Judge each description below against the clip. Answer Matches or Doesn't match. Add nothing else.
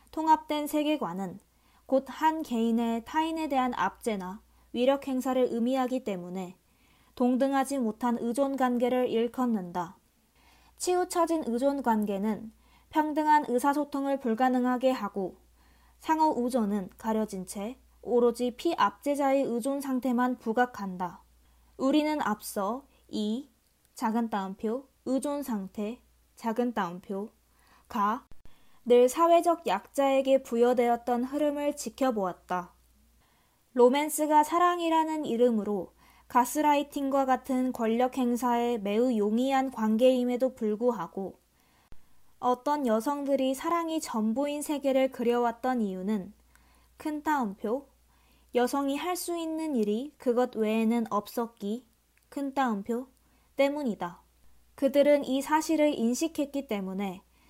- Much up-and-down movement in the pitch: Doesn't match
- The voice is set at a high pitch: Matches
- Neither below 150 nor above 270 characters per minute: Matches